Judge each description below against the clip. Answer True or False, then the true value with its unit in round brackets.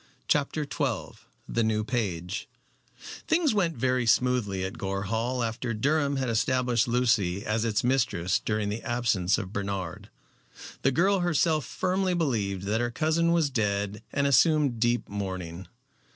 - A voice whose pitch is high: False (120 Hz)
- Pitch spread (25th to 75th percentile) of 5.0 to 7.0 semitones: True (5.5 semitones)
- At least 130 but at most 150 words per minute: True (145 wpm)